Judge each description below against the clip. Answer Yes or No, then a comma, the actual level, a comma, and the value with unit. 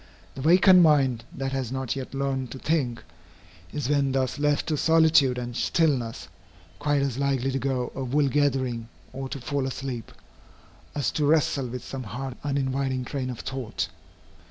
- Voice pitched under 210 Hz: Yes, low, 135 Hz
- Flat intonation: Yes, narrow, 2.1 semitones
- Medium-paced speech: Yes, average, 165 wpm